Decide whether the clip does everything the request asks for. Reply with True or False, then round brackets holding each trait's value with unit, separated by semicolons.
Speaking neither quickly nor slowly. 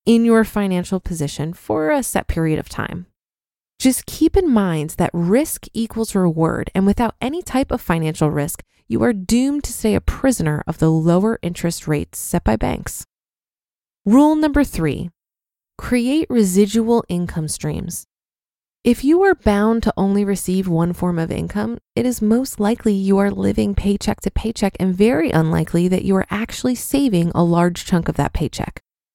True (170 wpm)